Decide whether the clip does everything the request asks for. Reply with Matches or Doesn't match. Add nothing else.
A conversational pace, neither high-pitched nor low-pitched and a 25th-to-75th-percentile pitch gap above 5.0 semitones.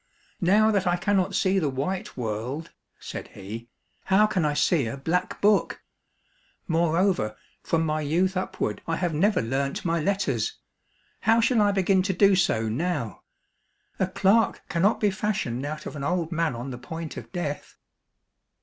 Matches